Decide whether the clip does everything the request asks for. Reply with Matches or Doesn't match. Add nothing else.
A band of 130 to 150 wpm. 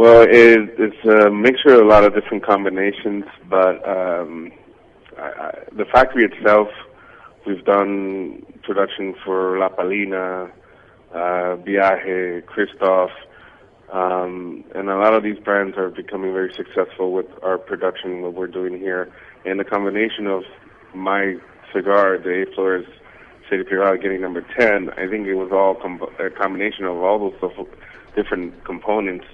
Matches